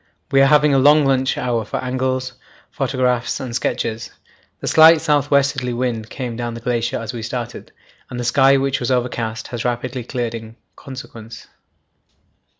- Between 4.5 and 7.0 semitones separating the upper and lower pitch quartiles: No, narrow, 2.5 semitones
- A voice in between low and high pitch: No, low, 125 Hz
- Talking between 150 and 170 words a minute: Yes, average, 165 wpm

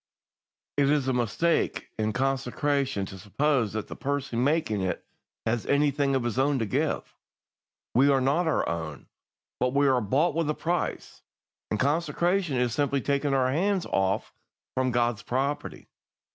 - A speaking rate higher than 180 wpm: No, average, 160 wpm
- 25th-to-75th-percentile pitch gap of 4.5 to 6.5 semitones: No, average, 3.5 semitones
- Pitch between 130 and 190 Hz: Yes, low, 135 Hz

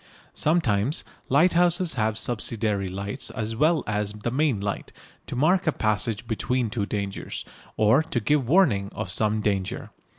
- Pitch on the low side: Yes, low, 115 Hz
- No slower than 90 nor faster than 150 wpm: Yes, average, 145 wpm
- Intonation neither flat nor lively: No, wide, 6.4 semitones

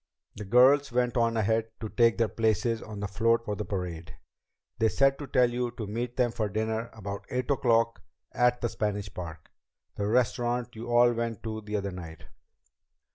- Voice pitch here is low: Yes, low, 115 Hz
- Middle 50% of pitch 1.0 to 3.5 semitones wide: Yes, average, 2.7 semitones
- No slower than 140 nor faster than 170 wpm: No, average, 185 wpm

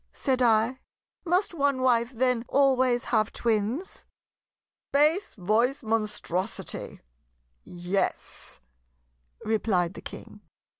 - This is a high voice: Yes, high, 235 Hz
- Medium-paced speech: No, slow, 90 wpm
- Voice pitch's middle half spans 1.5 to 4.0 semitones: Yes, average, 3.7 semitones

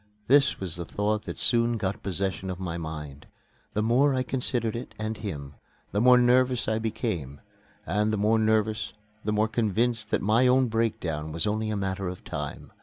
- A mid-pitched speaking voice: No, low, 110 Hz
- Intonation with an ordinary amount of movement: Yes, average, 3.7 semitones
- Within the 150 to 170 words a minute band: No, average, 185 wpm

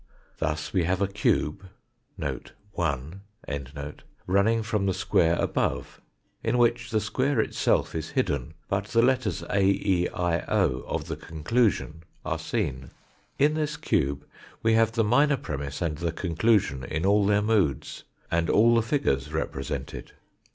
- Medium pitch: No, very low, 95 Hz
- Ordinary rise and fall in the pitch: No, wide, 6.0 semitones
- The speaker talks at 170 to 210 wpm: No, average, 145 wpm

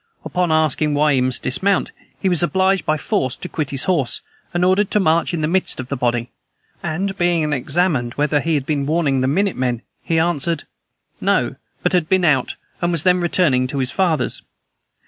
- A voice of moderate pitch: Yes, medium, 155 Hz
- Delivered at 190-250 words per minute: Yes, average, 200 wpm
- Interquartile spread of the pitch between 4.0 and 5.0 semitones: Yes, average, 4.5 semitones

